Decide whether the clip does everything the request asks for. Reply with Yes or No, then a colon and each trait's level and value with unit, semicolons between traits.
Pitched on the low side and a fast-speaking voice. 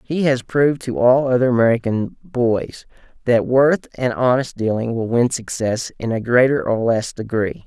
No: low, 120 Hz; average, 170 wpm